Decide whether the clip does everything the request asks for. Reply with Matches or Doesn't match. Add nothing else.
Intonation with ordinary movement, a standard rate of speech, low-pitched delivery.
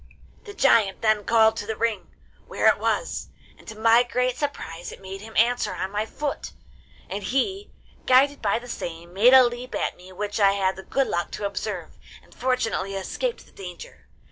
Doesn't match